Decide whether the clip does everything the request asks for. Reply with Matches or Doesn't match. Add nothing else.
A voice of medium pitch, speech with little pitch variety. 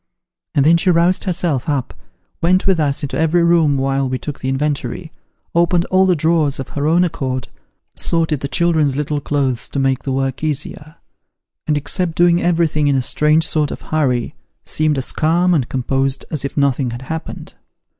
Doesn't match